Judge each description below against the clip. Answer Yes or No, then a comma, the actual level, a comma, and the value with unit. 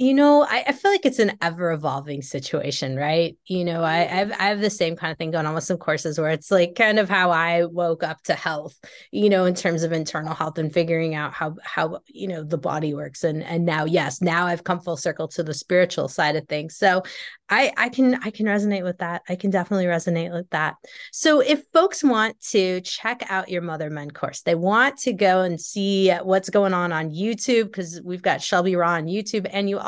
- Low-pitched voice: No, medium, 175 Hz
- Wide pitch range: No, average, 3.7 semitones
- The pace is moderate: No, fast, 235 wpm